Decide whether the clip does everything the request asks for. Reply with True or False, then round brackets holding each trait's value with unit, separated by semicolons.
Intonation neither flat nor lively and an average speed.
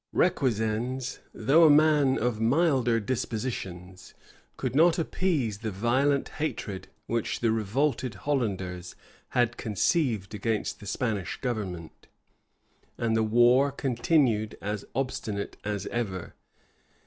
False (4.3 semitones; 110 wpm)